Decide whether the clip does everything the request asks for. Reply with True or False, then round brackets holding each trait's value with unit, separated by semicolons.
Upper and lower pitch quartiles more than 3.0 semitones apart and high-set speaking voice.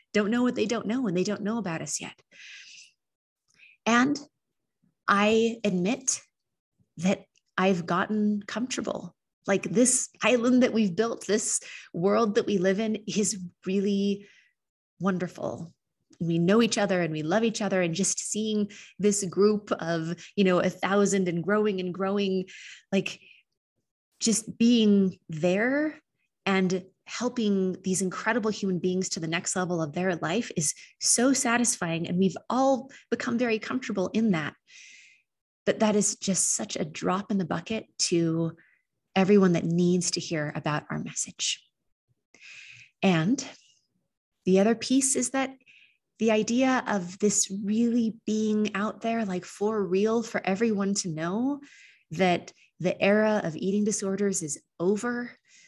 True (3.5 semitones; 200 Hz)